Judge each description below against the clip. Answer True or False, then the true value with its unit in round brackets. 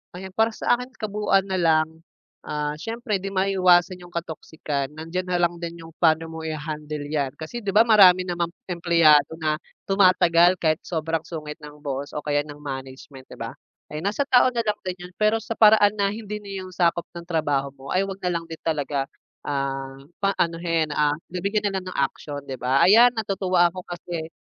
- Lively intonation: False (4.1 semitones)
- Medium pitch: True (170 Hz)